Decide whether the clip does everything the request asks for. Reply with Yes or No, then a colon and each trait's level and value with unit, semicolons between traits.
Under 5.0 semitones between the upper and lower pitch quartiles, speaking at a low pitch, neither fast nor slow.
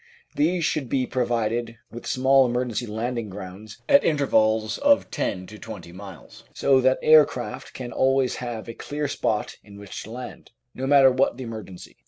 Yes: average, 3.5 semitones; low, 120 Hz; average, 175 wpm